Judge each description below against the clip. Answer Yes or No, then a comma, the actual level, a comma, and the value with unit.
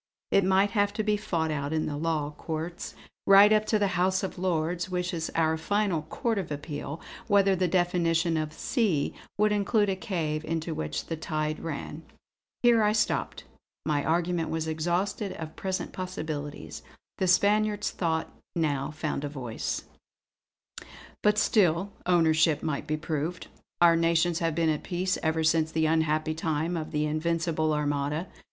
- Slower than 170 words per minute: Yes, average, 160 wpm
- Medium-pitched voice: Yes, medium, 165 Hz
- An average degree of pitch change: Yes, average, 3.2 semitones